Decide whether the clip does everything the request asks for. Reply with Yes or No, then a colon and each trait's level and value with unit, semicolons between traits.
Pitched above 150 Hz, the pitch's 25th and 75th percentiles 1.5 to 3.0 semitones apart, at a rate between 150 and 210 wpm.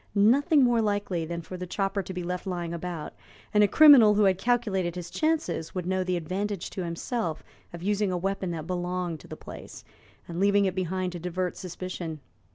Yes: medium, 185 Hz; average, 2.7 semitones; average, 200 wpm